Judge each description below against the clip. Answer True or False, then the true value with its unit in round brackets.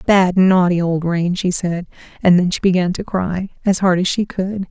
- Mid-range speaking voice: True (180 Hz)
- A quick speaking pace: True (215 wpm)